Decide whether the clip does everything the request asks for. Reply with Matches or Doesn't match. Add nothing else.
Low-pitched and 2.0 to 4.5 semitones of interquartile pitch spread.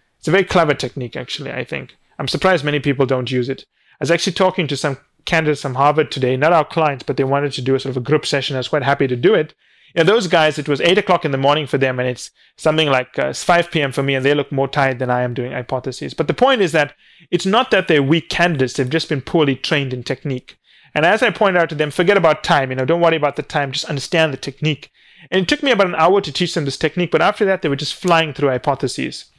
Doesn't match